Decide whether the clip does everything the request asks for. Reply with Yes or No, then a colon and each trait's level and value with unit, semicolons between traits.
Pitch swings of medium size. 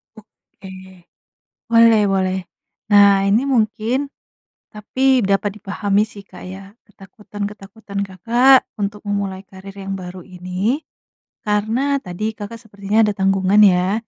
No: narrow, 2.2 semitones